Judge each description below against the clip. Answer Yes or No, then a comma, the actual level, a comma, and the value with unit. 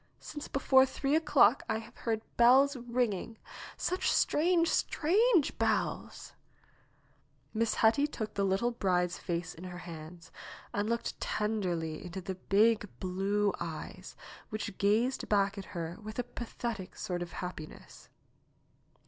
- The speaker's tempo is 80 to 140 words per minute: Yes, slow, 135 wpm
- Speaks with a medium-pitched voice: No, high, 215 Hz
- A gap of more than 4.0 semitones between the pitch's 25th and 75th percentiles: Yes, average, 5.1 semitones